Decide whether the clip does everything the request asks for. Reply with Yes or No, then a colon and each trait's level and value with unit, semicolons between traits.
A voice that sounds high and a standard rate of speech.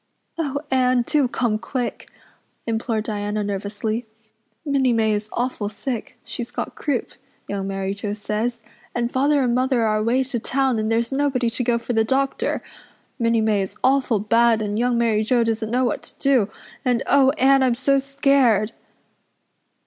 Yes: high, 235 Hz; average, 170 wpm